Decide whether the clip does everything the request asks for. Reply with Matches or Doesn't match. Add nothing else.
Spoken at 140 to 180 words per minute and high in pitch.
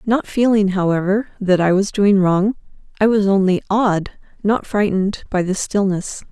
Matches